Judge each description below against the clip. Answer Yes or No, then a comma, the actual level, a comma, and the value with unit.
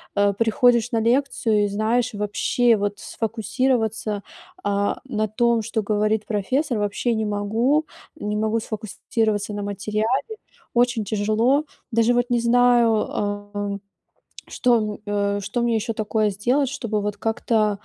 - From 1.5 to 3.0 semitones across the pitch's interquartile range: Yes, narrow, 2.5 semitones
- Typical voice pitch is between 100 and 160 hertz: No, high, 220 Hz